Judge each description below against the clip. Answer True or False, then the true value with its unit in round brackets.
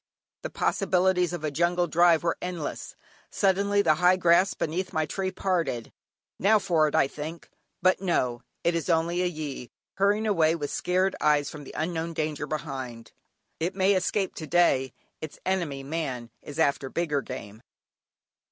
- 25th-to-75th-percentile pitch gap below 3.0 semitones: False (3.6 semitones)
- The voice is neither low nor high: True (165 Hz)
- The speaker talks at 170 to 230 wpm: False (160 wpm)